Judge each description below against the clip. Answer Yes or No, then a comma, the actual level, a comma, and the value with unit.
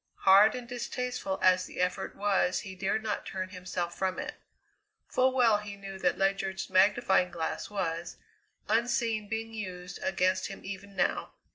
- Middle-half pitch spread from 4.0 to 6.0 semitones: No, average, 2.7 semitones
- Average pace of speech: Yes, average, 155 wpm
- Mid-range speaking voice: No, high, 195 Hz